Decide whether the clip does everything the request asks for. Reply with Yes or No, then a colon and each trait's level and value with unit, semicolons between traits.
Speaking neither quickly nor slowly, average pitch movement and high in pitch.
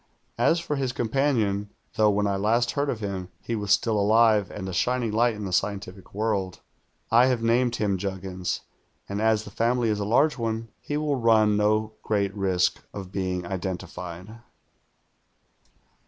No: average, 170 wpm; average, 3.0 semitones; low, 105 Hz